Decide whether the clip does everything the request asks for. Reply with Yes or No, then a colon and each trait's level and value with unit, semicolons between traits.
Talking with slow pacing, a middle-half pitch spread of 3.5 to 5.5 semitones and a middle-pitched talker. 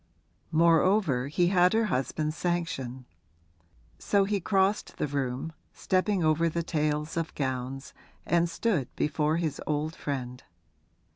Yes: slow, 125 wpm; average, 4.0 semitones; medium, 160 Hz